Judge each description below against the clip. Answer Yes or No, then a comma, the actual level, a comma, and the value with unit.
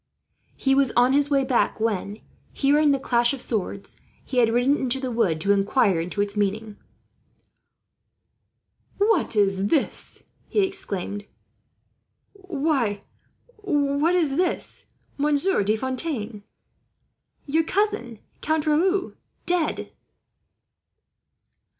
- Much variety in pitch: Yes, wide, 6.5 semitones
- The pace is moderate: No, slow, 110 wpm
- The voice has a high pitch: Yes, very high, 265 Hz